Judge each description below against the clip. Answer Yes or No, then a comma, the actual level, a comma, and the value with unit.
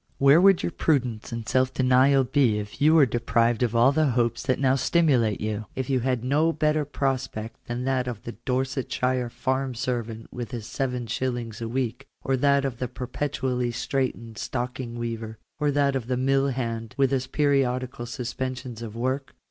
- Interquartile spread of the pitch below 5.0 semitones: Yes, narrow, 2.4 semitones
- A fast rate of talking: No, average, 180 wpm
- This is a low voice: Yes, low, 125 Hz